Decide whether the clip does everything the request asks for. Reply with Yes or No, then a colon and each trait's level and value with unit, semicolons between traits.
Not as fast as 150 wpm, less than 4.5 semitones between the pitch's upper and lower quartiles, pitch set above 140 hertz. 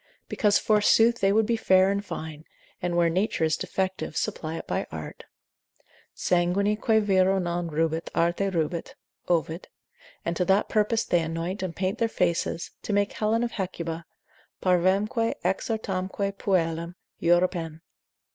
Yes: slow, 135 wpm; average, 3.3 semitones; medium, 185 Hz